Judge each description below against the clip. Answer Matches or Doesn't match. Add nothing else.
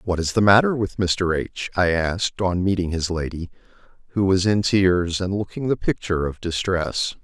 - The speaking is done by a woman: Doesn't match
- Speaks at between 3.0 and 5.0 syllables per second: Matches